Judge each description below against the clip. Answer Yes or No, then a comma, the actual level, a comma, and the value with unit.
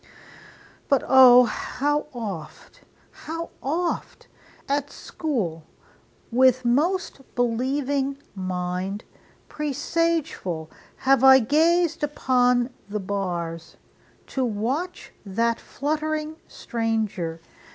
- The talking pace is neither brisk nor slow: No, slow, 80 wpm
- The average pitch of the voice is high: Yes, very high, 255 Hz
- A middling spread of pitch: No, wide, 6.2 semitones